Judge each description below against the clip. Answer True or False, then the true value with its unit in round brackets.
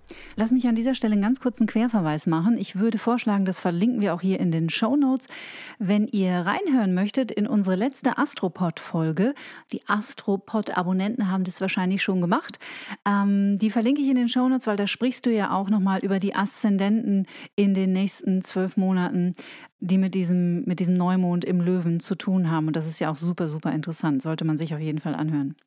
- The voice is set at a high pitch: True (195 Hz)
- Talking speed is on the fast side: True (210 wpm)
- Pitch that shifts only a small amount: False (3.9 semitones)